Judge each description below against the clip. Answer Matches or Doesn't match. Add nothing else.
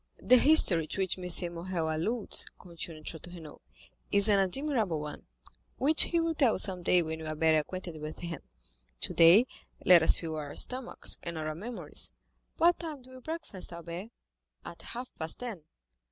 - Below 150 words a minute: Doesn't match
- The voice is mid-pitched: Matches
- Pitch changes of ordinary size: Doesn't match